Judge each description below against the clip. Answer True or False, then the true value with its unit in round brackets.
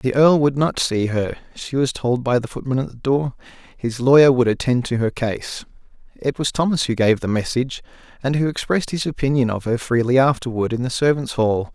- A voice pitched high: False (130 Hz)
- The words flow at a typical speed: False (215 wpm)